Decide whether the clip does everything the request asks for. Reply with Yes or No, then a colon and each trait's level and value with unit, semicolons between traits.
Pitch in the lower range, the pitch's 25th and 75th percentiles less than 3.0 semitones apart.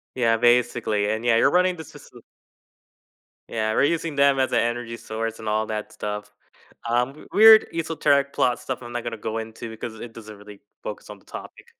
No: low, 115 Hz; average, 3.7 semitones